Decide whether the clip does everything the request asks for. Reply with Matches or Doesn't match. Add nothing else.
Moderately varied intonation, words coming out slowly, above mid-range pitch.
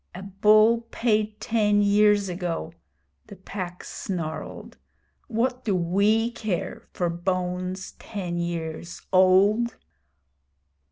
Matches